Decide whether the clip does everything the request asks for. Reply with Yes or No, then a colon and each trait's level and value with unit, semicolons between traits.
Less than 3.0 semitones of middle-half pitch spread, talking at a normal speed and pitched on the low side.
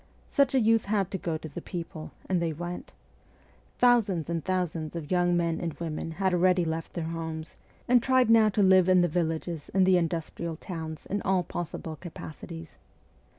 No: narrow, 2.5 semitones; average, 185 wpm; medium, 175 Hz